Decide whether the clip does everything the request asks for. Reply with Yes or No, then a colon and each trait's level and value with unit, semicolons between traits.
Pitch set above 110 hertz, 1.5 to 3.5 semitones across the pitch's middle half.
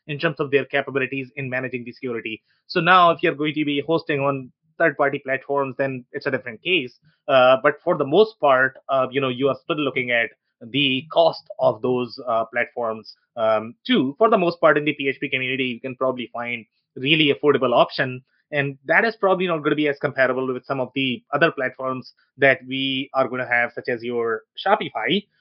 Yes: low, 135 Hz; average, 3.0 semitones